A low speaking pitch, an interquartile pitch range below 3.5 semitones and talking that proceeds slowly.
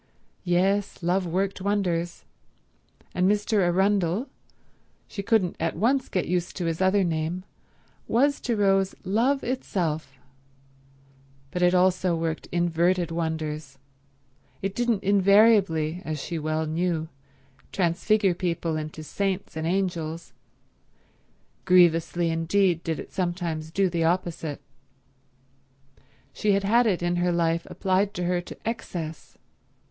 No: medium, 180 Hz; average, 3.0 semitones; slow, 120 wpm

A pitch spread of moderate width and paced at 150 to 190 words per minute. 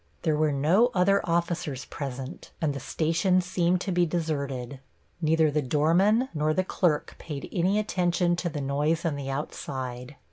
Yes: average, 3.9 semitones; average, 165 wpm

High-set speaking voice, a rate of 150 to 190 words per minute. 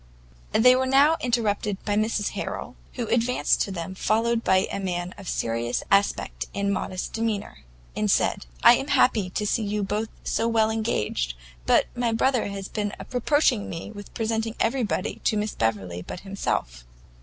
Yes: high, 210 Hz; average, 175 wpm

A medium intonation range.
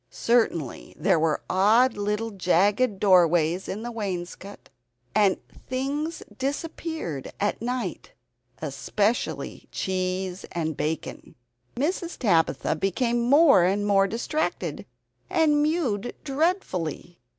No: wide, 6.0 semitones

